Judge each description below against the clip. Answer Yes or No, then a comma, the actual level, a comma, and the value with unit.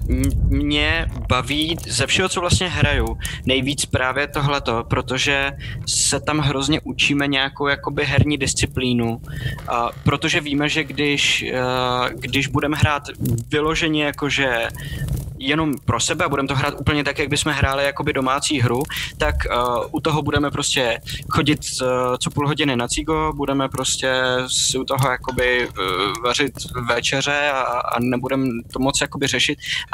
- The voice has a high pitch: No, medium, 140 Hz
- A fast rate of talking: No, average, 140 wpm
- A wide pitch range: No, narrow, 2.5 semitones